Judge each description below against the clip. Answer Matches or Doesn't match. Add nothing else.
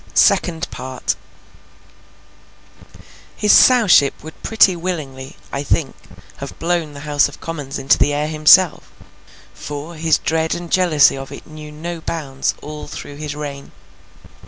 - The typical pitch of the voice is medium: Matches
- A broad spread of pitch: Doesn't match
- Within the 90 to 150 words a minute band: Matches